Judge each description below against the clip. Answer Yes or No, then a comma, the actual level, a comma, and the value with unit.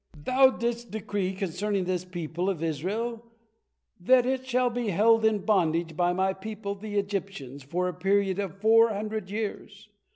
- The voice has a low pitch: No, high, 200 Hz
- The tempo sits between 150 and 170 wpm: Yes, average, 160 wpm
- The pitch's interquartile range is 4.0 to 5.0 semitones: No, average, 3.3 semitones